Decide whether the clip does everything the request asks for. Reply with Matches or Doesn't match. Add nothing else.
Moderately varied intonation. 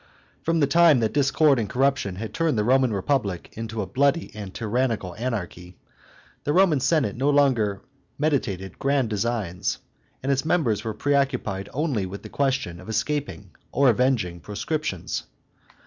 Doesn't match